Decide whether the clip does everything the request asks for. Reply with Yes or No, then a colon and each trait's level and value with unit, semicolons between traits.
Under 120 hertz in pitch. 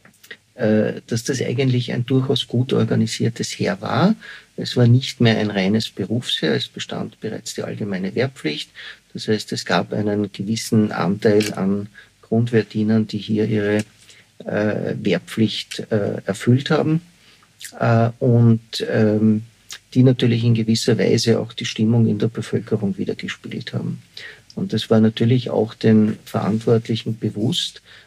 Yes: low, 110 Hz